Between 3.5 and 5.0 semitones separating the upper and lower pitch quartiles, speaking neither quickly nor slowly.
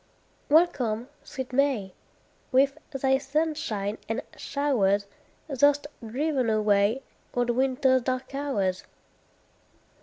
No: average, 4.3 semitones; slow, 90 wpm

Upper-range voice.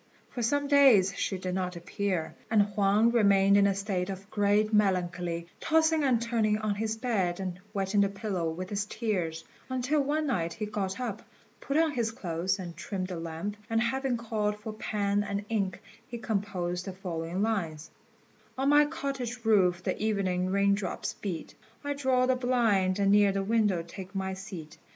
Yes: high, 200 Hz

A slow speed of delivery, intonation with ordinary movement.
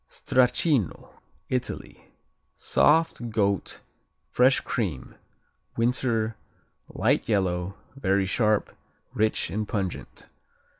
Yes: slow, 80 wpm; average, 4.1 semitones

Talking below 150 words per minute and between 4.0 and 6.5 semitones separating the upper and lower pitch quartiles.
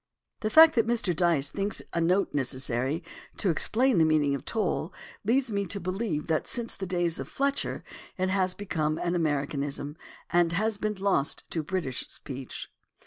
No: average, 175 wpm; average, 5.2 semitones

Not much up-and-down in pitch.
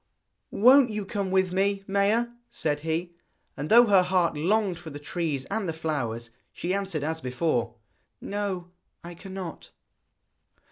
No: average, 4.0 semitones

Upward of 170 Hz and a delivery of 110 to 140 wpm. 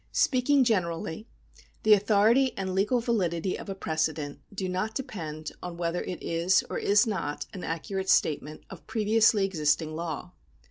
No: high, 190 Hz; average, 150 wpm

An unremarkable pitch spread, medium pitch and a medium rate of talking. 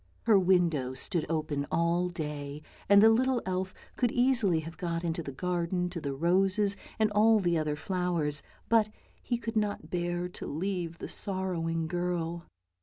Yes: average, 3.2 semitones; medium, 175 Hz; average, 165 wpm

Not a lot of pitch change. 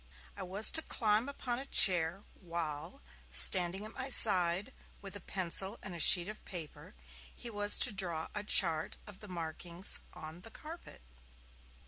No: average, 3.7 semitones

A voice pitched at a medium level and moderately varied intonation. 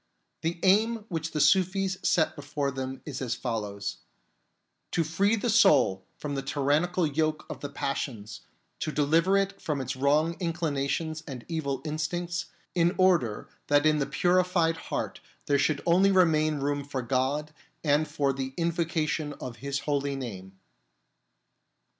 Yes: medium, 150 Hz; average, 3.6 semitones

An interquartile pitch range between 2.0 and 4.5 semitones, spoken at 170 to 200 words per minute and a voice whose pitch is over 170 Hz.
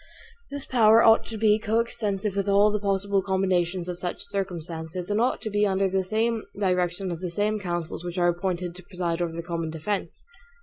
Yes: average, 3.1 semitones; average, 190 wpm; high, 190 Hz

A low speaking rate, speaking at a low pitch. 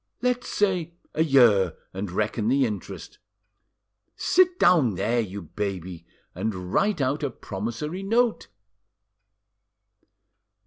Yes: slow, 105 wpm; low, 120 Hz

